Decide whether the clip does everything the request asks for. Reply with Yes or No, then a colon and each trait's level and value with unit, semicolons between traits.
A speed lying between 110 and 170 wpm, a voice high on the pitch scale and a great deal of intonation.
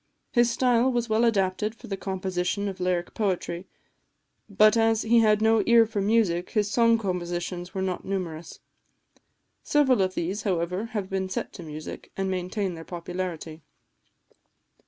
No: average, 155 wpm; high, 195 Hz; average, 3.7 semitones